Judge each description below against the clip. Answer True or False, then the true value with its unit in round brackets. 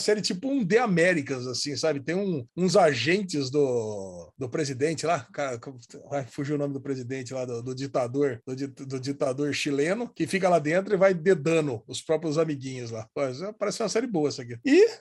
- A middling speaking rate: False (190 wpm)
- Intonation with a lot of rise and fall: True (5.7 semitones)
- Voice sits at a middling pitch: True (150 Hz)